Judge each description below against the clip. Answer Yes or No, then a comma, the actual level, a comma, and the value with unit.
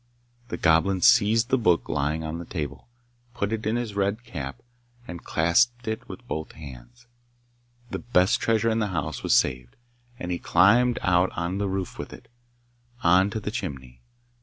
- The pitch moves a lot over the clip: Yes, wide, 5.7 semitones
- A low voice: Yes, very low, 90 Hz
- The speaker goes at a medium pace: Yes, average, 180 wpm